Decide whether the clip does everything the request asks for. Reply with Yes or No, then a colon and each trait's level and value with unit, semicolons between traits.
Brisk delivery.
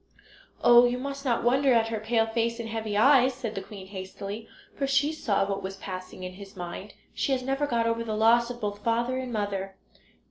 Yes: fast, 215 wpm